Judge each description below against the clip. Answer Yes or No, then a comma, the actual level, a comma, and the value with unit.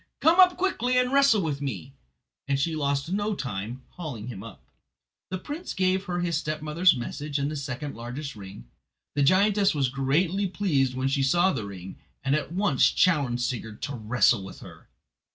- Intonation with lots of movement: Yes, wide, 6.7 semitones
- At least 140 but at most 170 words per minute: No, average, 185 wpm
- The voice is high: No, medium, 145 Hz